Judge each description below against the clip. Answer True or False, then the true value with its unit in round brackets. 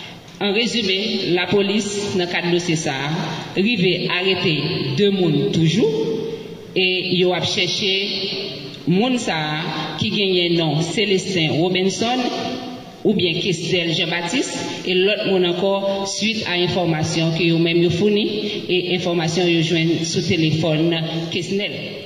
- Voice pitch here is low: False (180 Hz)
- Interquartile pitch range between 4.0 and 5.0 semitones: False (2.9 semitones)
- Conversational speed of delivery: False (130 wpm)